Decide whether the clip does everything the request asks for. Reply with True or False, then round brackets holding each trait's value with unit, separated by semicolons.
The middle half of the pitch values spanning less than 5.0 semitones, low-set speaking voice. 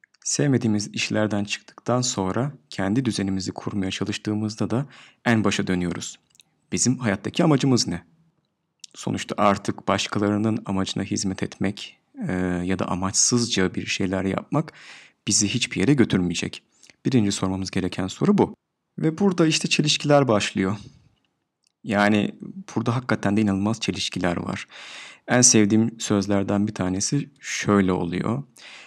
True (4.3 semitones; 105 Hz)